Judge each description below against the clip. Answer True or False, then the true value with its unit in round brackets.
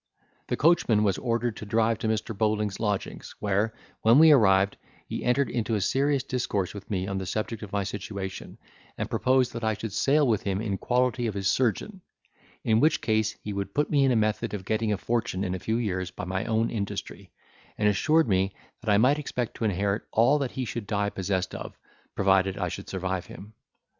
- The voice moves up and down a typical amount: True (3.4 semitones)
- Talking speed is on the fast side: True (210 wpm)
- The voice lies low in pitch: True (110 Hz)